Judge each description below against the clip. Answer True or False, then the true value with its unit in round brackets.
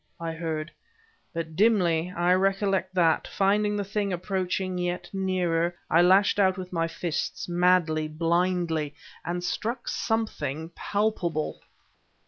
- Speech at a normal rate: False (120 wpm)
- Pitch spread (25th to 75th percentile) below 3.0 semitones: True (2.6 semitones)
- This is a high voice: False (180 Hz)